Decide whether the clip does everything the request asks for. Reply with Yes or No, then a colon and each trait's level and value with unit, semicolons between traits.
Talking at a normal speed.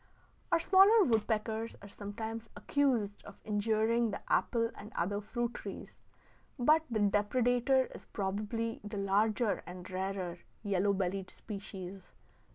No: slow, 125 wpm